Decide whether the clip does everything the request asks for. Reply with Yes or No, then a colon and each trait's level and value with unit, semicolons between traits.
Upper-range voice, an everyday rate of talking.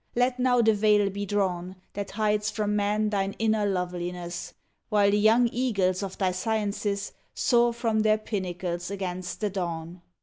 Yes: high, 205 Hz; average, 160 wpm